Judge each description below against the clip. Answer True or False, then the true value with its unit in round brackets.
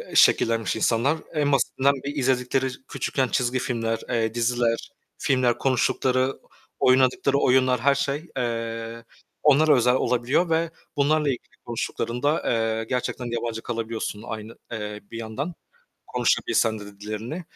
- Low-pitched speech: True (125 Hz)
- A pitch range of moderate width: True (3.0 semitones)